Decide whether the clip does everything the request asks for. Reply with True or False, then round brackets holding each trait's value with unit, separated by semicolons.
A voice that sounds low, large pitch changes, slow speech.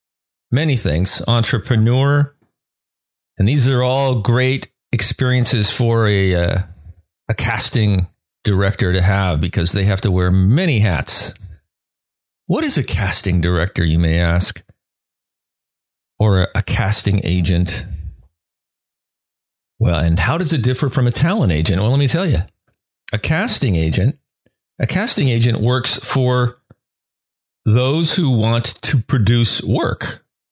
True (105 Hz; 5.8 semitones; 130 wpm)